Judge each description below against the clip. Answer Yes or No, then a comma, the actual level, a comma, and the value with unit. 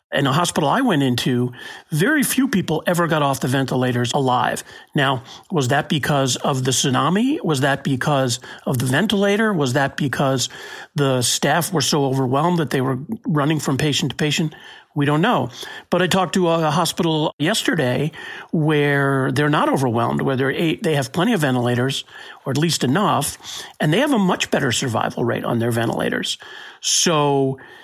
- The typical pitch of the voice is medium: Yes, medium, 145 Hz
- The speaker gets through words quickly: No, average, 175 wpm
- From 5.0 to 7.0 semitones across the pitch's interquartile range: No, average, 3.6 semitones